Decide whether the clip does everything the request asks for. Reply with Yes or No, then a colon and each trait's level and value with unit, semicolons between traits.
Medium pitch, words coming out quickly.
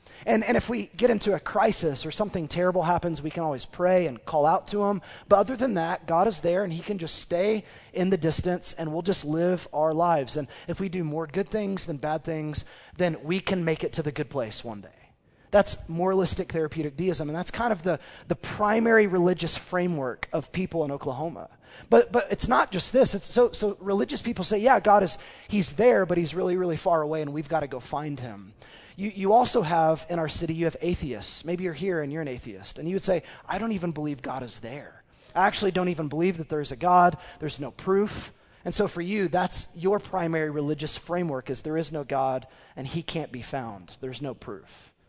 Yes: medium, 170 Hz; fast, 230 wpm